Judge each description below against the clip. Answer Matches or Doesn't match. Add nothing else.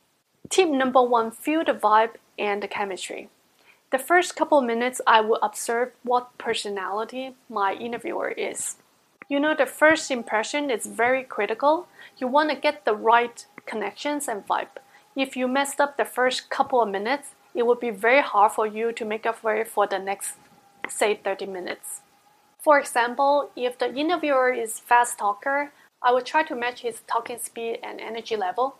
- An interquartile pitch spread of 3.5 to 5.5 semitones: Matches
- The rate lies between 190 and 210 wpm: Doesn't match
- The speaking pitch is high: Matches